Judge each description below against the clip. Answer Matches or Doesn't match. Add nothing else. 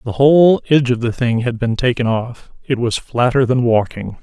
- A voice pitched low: Matches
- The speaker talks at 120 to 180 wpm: Doesn't match